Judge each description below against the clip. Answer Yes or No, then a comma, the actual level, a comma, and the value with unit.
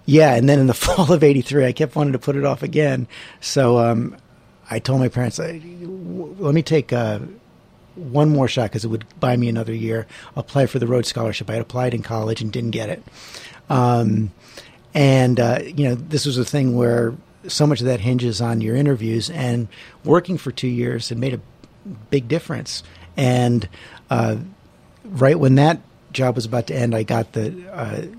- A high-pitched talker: No, low, 125 Hz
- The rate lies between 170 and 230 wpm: Yes, average, 195 wpm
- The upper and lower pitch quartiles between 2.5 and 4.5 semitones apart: Yes, average, 3.8 semitones